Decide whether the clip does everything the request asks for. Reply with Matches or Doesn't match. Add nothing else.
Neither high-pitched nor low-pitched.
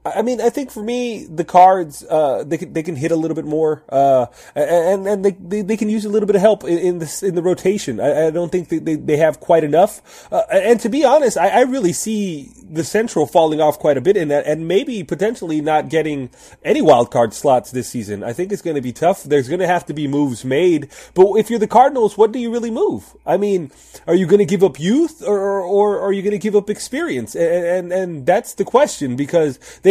Matches